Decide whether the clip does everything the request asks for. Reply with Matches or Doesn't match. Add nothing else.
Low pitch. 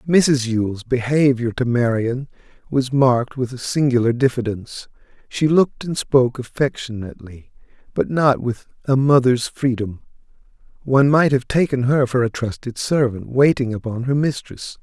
Matches